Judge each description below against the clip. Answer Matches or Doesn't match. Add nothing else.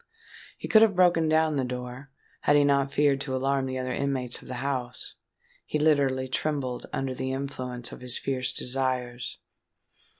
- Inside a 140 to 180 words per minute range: Matches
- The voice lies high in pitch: Doesn't match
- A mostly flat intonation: Matches